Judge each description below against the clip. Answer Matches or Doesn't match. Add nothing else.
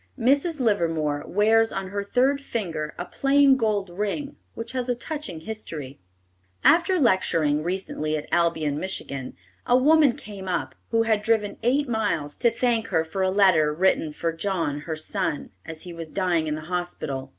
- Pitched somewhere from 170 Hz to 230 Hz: Matches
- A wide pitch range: Matches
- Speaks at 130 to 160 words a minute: Doesn't match